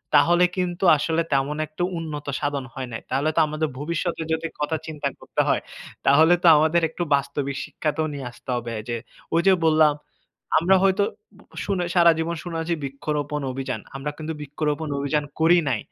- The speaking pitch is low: No, medium, 155 Hz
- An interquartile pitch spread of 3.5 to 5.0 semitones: No, average, 2.7 semitones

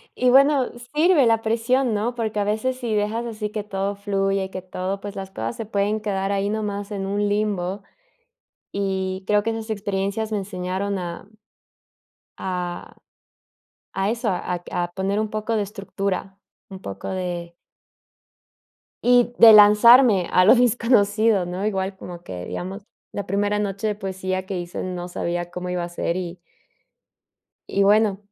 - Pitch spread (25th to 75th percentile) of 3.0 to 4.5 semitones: No, narrow, 2.5 semitones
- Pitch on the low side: No, high, 200 Hz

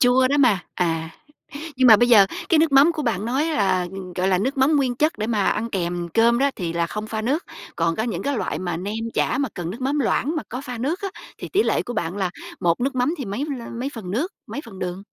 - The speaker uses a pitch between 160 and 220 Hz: No, high, 230 Hz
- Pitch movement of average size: No, wide, 6.4 semitones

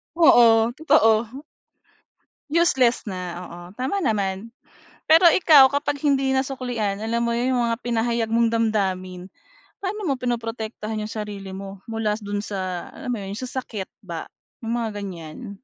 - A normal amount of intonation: Yes, average, 4.1 semitones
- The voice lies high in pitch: Yes, high, 230 Hz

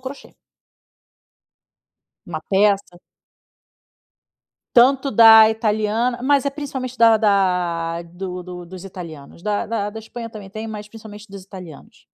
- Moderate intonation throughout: Yes, average, 3.9 semitones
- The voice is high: Yes, high, 210 Hz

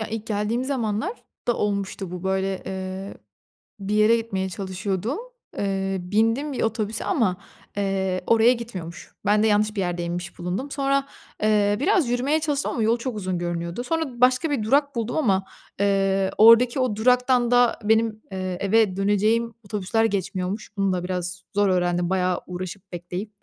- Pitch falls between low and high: No, high, 210 Hz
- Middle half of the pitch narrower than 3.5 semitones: No, average, 3.8 semitones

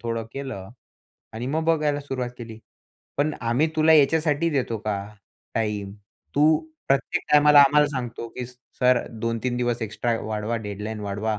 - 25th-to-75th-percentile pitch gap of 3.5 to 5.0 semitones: Yes, average, 4.5 semitones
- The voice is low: Yes, low, 120 Hz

